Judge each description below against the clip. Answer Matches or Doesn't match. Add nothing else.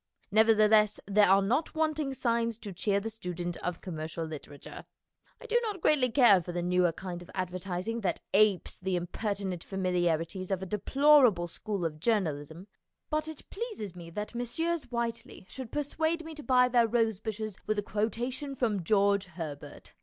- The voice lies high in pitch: Matches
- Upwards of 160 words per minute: Matches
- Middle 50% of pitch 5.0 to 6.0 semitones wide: Matches